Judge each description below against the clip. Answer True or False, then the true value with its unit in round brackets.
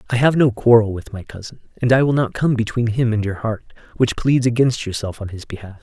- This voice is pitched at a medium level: False (115 Hz)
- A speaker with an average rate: False (235 wpm)